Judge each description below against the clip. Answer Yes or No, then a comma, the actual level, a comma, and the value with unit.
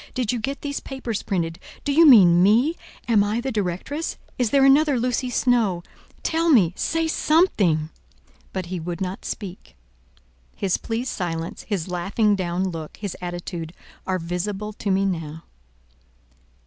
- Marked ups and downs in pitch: Yes, wide, 6.2 semitones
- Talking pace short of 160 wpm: Yes, average, 150 wpm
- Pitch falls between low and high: No, high, 200 Hz